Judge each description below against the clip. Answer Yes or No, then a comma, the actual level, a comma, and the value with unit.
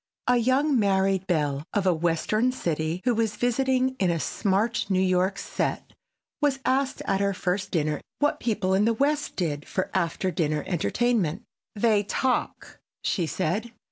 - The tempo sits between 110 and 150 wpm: No, average, 160 wpm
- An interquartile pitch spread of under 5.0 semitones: No, wide, 5.4 semitones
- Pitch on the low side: No, high, 195 Hz